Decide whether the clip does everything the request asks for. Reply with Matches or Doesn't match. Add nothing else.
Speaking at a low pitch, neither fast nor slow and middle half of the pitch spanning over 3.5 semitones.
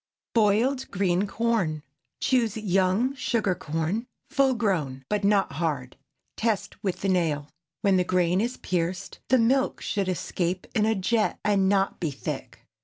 Doesn't match